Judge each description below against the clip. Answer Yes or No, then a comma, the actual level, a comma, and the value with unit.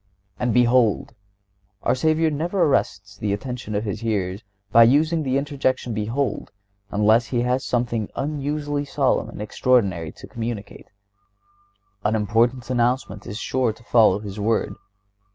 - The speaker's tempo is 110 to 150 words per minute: Yes, average, 140 wpm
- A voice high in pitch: No, low, 120 Hz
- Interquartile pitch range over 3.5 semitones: Yes, average, 4.1 semitones